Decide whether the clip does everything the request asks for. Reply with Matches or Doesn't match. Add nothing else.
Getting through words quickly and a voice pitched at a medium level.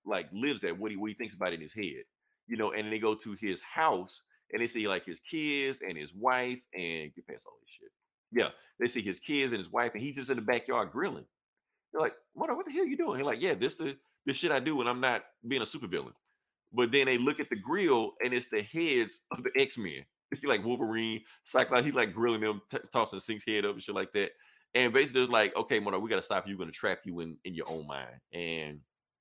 Doesn't match